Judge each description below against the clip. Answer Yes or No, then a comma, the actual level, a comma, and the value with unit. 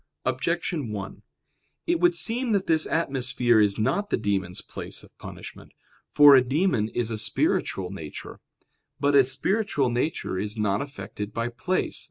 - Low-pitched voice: Yes, low, 130 Hz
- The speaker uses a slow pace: No, average, 155 wpm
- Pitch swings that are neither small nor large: No, wide, 7.5 semitones